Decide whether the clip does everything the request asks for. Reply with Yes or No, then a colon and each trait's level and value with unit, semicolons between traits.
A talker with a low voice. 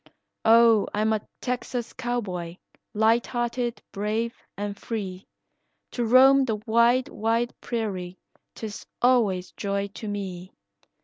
No: high, 225 Hz